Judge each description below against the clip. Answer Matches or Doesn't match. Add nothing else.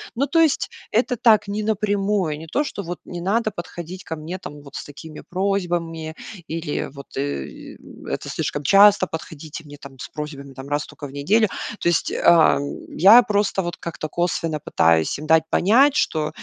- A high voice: Doesn't match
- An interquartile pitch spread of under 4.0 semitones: Doesn't match